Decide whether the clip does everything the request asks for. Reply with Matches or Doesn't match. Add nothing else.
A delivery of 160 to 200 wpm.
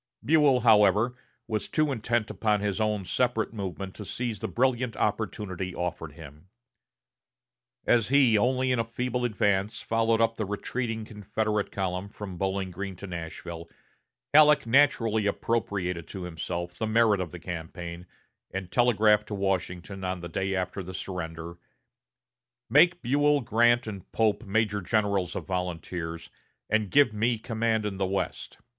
Doesn't match